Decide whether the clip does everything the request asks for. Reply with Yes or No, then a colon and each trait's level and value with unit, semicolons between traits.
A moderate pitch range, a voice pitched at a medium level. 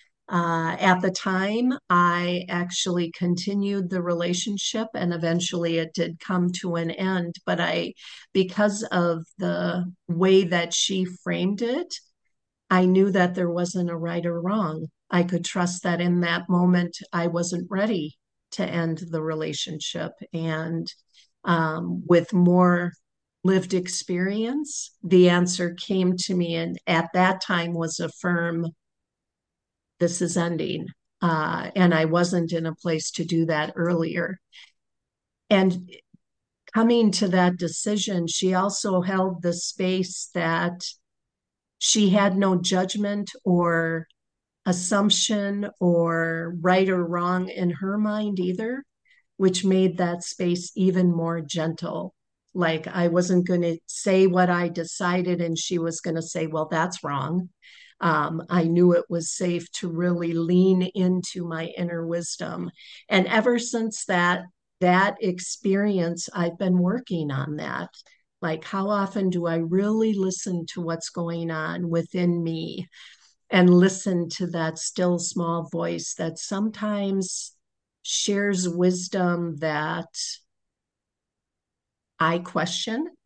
No: narrow, 2.1 semitones; medium, 175 Hz